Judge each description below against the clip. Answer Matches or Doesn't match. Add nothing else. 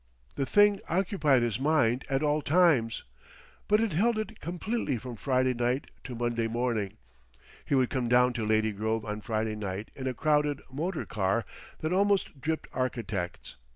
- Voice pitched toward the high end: Doesn't match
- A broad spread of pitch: Matches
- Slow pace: Doesn't match